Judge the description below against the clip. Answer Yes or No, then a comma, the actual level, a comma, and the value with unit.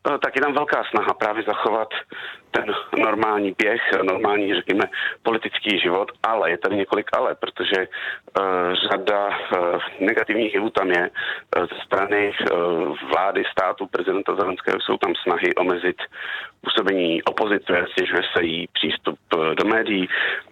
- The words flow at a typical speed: Yes, average, 125 wpm